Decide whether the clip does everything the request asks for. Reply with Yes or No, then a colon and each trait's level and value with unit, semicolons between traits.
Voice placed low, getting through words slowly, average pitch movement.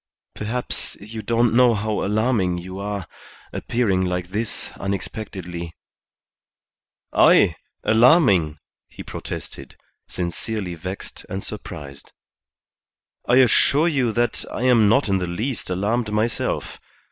Yes: low, 105 Hz; slow, 115 wpm; average, 4.3 semitones